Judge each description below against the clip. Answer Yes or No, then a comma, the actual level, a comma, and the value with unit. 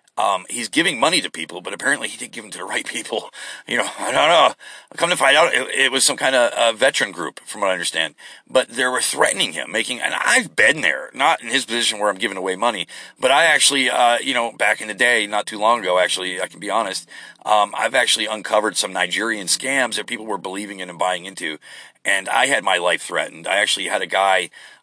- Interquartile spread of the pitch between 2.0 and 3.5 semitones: Yes, narrow, 2.5 semitones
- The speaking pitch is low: Yes, very low, 95 Hz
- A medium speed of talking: No, fast, 245 wpm